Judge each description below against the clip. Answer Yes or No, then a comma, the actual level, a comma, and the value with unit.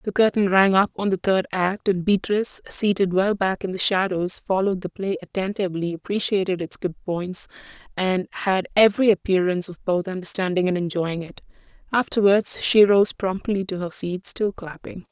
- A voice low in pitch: No, high, 190 Hz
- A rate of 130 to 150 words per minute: No, average, 170 wpm